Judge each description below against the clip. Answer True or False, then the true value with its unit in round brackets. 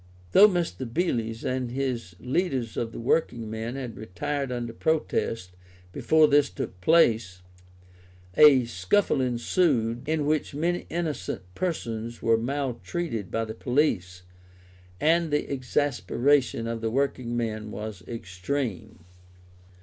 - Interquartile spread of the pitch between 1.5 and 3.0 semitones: False (4.6 semitones)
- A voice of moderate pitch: False (125 Hz)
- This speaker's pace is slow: True (120 wpm)